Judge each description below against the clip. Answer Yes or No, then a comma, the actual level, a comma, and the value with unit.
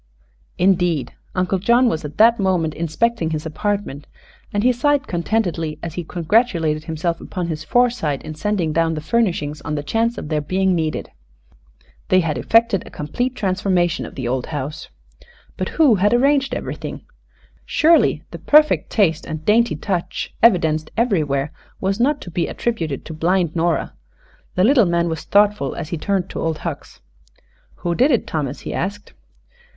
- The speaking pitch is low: No, medium, 175 Hz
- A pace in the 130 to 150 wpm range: No, average, 165 wpm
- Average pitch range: No, wide, 5.9 semitones